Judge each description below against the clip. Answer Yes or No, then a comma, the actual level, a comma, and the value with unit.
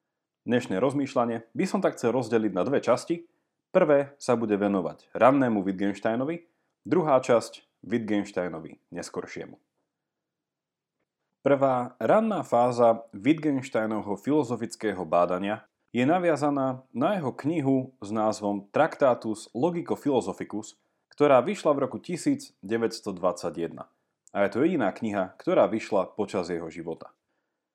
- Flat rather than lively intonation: No, wide, 6.3 semitones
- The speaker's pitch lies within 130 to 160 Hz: No, low, 120 Hz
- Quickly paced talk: No, slow, 110 wpm